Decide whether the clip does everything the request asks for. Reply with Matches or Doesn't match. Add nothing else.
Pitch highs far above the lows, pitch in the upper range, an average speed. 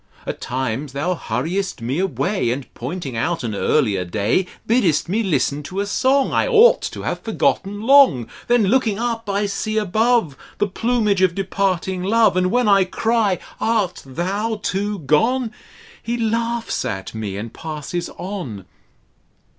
Matches